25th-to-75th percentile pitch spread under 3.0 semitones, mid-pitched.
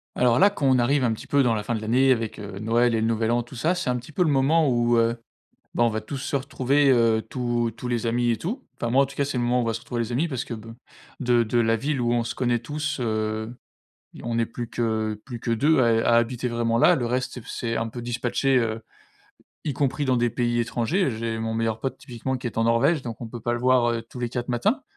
No: narrow, 2.4 semitones; low, 120 Hz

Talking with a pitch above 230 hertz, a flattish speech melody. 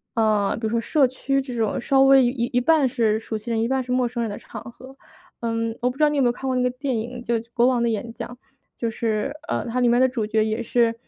Yes: high, 240 Hz; narrow, 2.2 semitones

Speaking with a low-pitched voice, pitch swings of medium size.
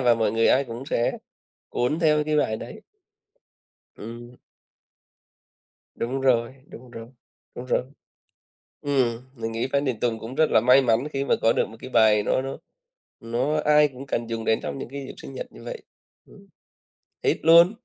Yes: low, 125 Hz; average, 3.5 semitones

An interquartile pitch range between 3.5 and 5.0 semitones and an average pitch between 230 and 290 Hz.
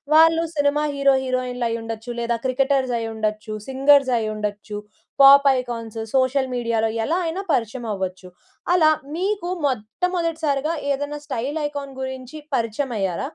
Yes: average, 4.2 semitones; very high, 260 Hz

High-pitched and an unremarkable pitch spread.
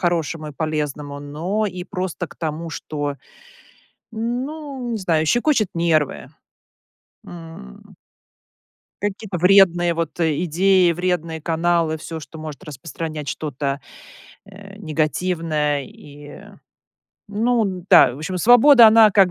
No: medium, 170 Hz; average, 4.2 semitones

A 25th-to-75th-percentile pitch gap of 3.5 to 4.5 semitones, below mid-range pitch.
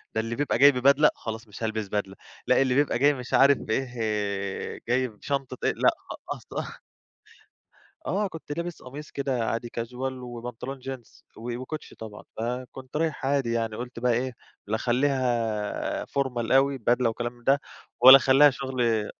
No: average, 2.8 semitones; low, 125 Hz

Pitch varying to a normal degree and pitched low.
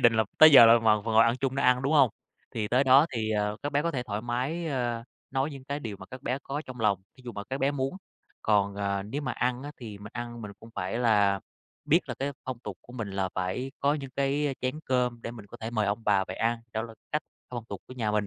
Yes: average, 3.9 semitones; low, 120 Hz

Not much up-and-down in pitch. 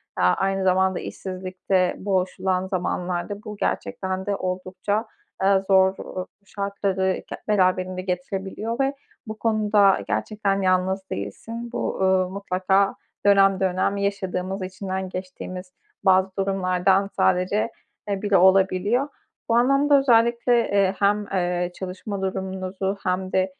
Yes: narrow, 1.5 semitones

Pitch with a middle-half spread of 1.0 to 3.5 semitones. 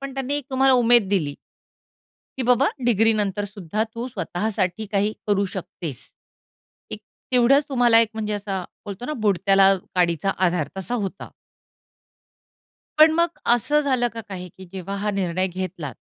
No: average, 4.4 semitones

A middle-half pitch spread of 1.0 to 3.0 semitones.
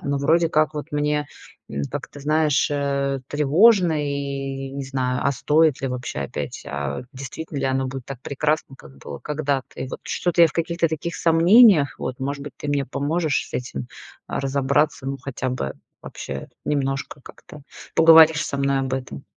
Yes: narrow, 2.5 semitones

